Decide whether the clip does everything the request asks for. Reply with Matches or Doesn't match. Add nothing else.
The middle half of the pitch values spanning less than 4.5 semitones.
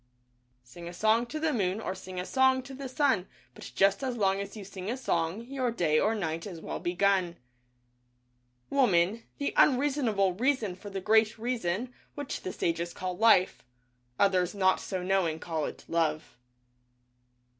Doesn't match